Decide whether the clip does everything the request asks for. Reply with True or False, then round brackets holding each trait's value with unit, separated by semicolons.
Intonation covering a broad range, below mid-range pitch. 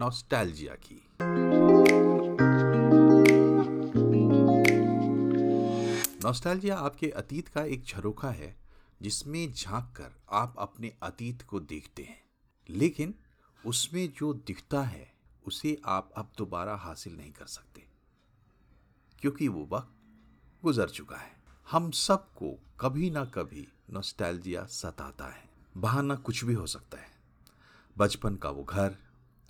True (7.6 semitones; 105 Hz)